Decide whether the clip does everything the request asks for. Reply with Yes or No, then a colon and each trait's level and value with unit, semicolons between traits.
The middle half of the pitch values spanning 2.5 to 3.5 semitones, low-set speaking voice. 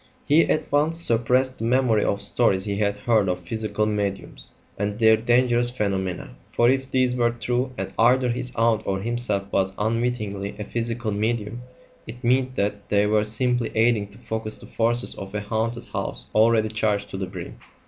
Yes: average, 2.9 semitones; low, 110 Hz